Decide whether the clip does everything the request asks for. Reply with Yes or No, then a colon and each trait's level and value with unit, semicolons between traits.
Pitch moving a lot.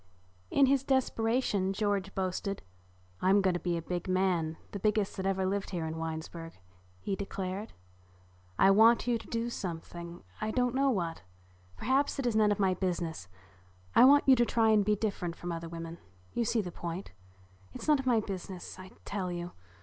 No: average, 4.2 semitones